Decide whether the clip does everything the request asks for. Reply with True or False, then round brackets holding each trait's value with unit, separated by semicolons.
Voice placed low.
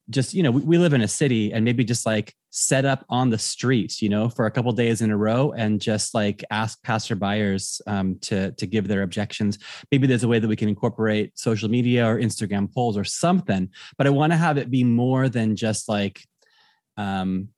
True (110 Hz)